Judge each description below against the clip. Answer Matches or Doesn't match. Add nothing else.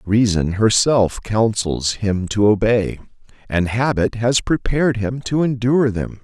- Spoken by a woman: Doesn't match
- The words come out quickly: Doesn't match